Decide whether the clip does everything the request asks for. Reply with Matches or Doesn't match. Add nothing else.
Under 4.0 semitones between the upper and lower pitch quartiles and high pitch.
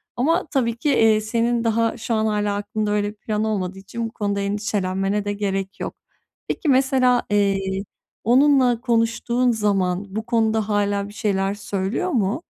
Matches